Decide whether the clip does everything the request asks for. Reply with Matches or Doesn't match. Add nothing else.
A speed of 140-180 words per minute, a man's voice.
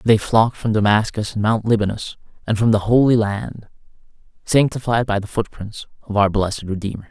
Matches